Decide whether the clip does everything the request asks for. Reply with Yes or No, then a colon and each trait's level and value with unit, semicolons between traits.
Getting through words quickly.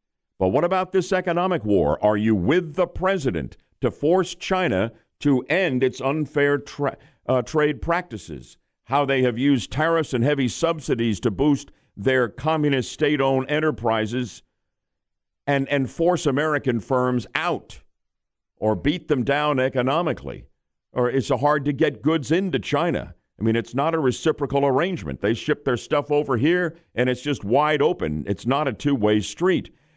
No: average, 155 wpm